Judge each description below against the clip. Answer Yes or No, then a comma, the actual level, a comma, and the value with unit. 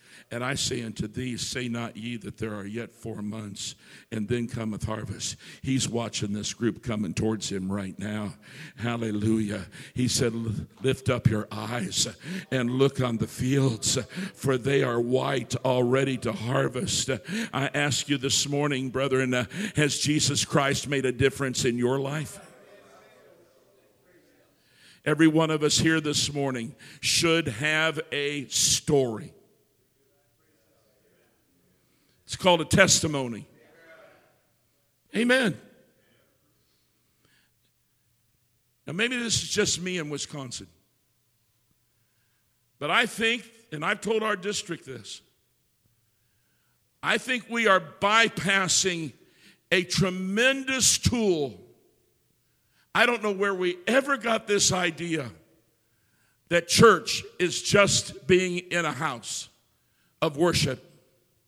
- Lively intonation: Yes, wide, 6.3 semitones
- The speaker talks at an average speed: No, slow, 120 wpm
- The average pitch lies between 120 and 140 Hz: Yes, low, 135 Hz